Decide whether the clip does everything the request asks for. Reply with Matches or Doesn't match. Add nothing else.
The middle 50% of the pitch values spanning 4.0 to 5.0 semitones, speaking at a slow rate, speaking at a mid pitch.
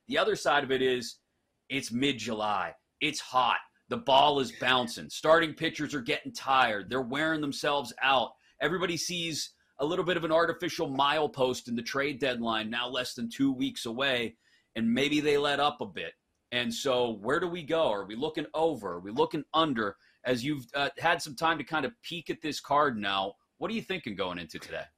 Doesn't match